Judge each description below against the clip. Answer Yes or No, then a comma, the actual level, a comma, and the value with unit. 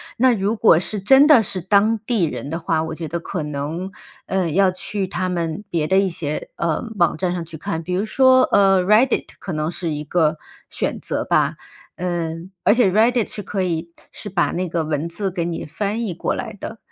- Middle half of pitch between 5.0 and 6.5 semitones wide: No, average, 3.7 semitones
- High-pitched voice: No, medium, 180 Hz